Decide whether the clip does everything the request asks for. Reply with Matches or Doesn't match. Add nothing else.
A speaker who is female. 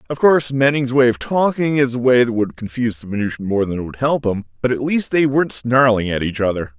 Doesn't match